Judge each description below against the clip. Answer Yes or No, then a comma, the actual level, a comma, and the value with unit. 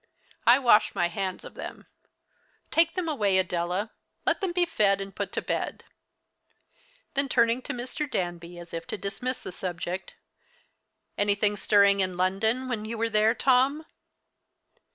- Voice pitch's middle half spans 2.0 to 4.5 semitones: No, average, 5.2 semitones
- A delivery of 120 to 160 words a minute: Yes, average, 155 wpm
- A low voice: No, high, 210 Hz